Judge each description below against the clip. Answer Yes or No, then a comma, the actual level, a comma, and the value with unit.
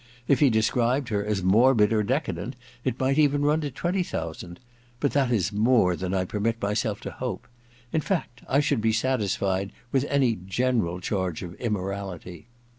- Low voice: Yes, low, 110 Hz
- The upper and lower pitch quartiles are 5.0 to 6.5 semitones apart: Yes, average, 5.3 semitones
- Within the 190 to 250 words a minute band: No, average, 180 wpm